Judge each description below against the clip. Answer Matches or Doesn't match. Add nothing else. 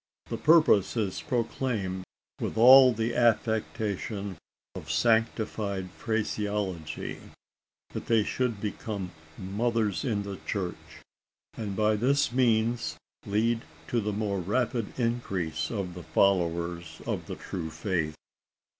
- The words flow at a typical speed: Doesn't match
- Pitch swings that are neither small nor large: Matches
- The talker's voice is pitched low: Matches